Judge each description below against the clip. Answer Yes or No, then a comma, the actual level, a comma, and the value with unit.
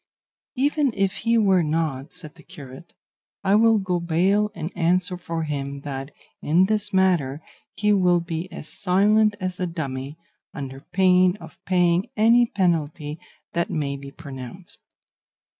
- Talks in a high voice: No, medium, 175 Hz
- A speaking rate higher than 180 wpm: No, average, 145 wpm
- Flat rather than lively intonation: No, average, 4.3 semitones